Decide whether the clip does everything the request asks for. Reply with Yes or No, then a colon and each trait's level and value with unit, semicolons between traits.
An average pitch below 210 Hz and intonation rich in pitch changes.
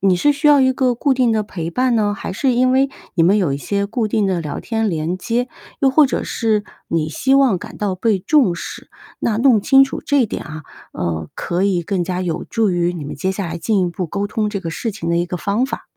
Yes: high, 200 Hz; wide, 5.9 semitones